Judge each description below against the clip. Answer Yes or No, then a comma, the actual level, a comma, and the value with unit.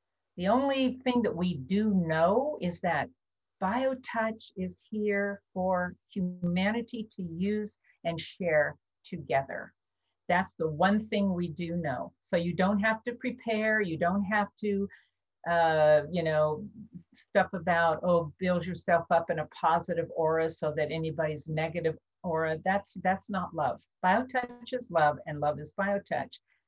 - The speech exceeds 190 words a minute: No, average, 145 wpm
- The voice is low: No, medium, 180 Hz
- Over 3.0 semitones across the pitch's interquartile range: Yes, average, 4.1 semitones